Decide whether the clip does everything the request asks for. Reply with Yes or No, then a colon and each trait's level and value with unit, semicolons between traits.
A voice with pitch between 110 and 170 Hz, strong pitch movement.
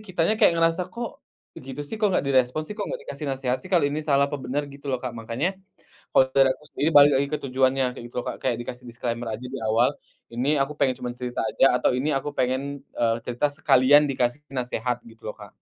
No: low, 135 Hz; average, 2.9 semitones